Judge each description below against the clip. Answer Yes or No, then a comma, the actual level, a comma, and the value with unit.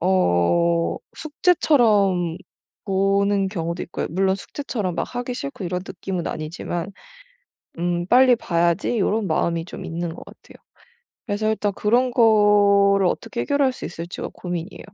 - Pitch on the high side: Yes, high, 195 Hz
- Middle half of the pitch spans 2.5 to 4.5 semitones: Yes, average, 4.0 semitones